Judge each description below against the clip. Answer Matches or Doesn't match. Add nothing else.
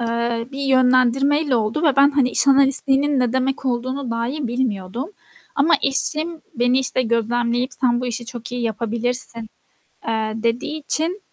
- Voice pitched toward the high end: Matches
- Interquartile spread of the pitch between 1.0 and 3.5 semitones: Matches